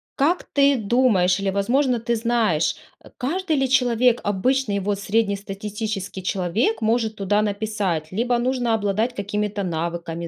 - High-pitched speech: Yes, high, 215 Hz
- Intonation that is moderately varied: Yes, average, 3.6 semitones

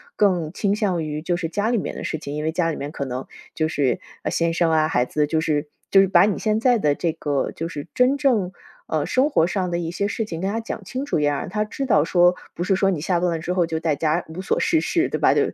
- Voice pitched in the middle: Yes, medium, 175 Hz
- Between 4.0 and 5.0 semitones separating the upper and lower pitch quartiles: Yes, average, 4.5 semitones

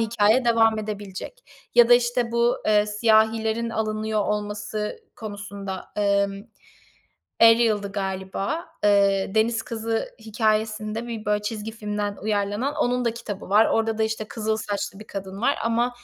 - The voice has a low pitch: No, high, 215 Hz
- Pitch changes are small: Yes, narrow, 1.8 semitones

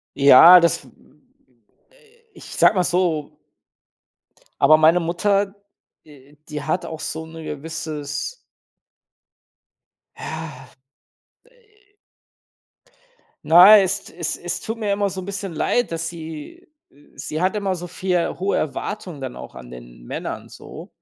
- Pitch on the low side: No, medium, 170 Hz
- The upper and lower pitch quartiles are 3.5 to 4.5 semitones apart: Yes, average, 4.2 semitones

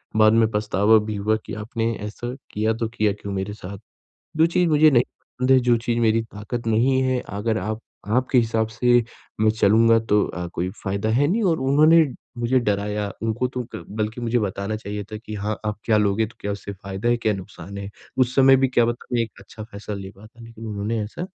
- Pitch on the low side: Yes, low, 110 Hz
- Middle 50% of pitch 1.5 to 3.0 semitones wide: Yes, average, 2.7 semitones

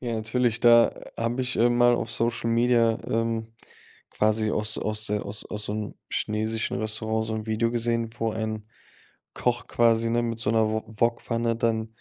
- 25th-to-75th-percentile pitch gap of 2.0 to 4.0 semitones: No, narrow, 1.2 semitones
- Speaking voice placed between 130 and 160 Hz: No, low, 115 Hz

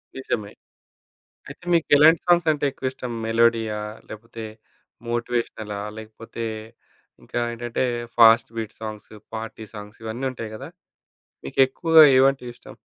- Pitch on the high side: No, low, 115 Hz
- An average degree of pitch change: Yes, average, 3.1 semitones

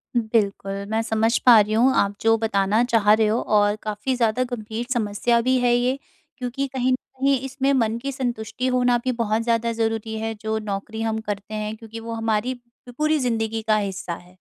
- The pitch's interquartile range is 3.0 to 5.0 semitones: No, narrow, 2.4 semitones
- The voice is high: Yes, high, 225 Hz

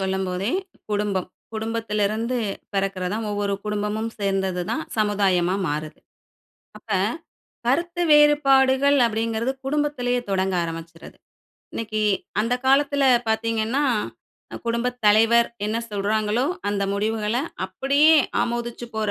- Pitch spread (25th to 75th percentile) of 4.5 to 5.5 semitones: No, average, 3.7 semitones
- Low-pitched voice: No, high, 220 Hz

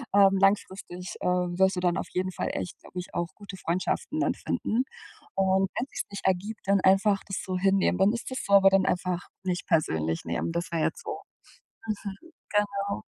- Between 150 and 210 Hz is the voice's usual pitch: Yes, high, 190 Hz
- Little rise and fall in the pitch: Yes, narrow, 1.8 semitones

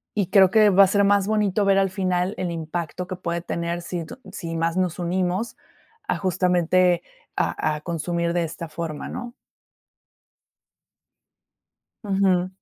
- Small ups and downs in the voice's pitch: Yes, narrow, 2.3 semitones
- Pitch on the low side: No, medium, 180 Hz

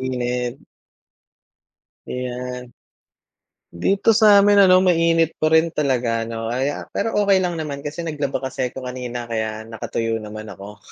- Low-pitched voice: Yes, low, 130 Hz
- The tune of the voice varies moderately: No, wide, 5.9 semitones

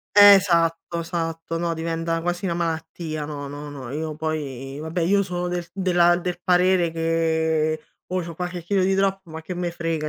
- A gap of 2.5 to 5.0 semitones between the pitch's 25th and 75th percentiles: No, narrow, 1.8 semitones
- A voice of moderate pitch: Yes, medium, 165 Hz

